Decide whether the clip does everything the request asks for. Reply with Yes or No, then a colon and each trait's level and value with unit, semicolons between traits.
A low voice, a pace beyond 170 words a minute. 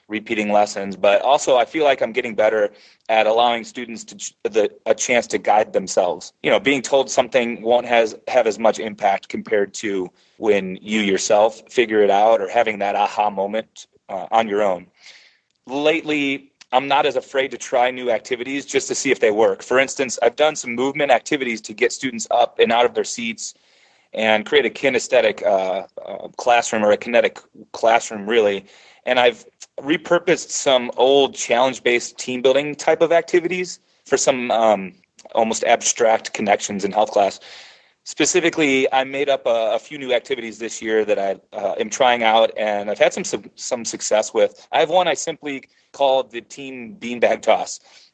Yes: low, 125 Hz; average, 185 wpm